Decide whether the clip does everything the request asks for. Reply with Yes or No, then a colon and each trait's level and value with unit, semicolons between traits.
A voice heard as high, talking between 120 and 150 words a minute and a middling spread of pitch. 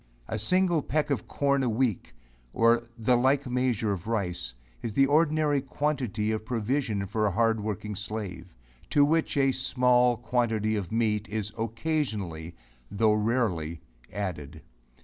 No: low, 115 Hz; average, 145 wpm; average, 4.0 semitones